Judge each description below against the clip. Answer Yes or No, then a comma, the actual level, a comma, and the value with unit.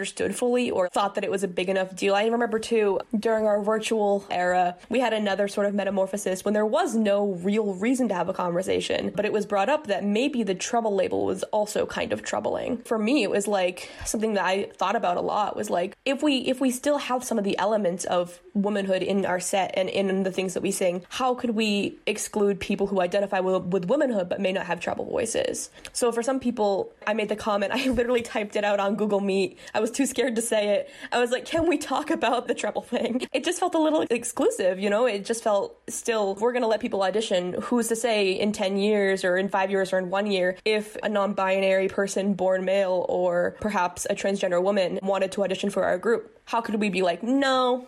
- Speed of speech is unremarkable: No, fast, 235 wpm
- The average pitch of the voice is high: Yes, high, 205 Hz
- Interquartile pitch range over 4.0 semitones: No, average, 3.7 semitones